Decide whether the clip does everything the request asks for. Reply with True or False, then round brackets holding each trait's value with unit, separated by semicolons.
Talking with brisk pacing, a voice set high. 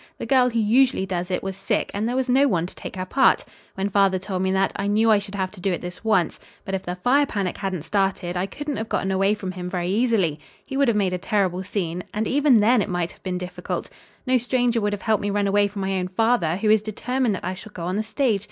True (275 wpm; 200 Hz)